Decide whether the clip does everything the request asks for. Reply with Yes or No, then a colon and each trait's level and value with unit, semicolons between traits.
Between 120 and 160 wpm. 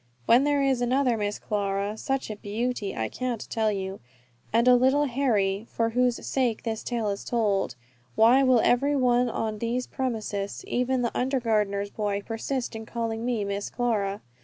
No: average, 175 wpm